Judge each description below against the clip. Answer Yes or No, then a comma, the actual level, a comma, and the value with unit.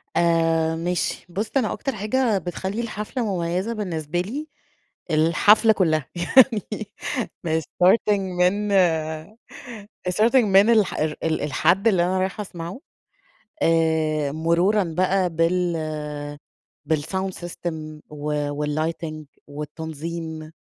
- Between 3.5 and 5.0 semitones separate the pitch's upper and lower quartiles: Yes, average, 4.2 semitones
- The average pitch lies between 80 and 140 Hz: No, medium, 175 Hz